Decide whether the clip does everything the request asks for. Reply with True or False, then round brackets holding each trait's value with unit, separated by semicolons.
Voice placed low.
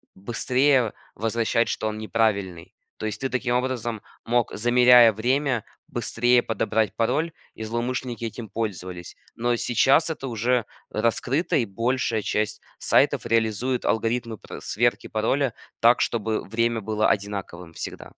True (115 Hz)